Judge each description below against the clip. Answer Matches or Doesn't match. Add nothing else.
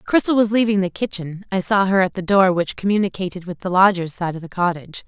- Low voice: Doesn't match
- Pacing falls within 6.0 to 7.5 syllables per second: Matches